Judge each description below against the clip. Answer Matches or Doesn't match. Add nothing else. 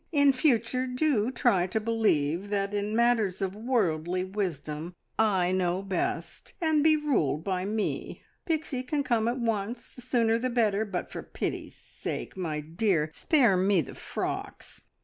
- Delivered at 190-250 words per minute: Doesn't match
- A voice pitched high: Matches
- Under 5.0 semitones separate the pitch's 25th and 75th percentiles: Doesn't match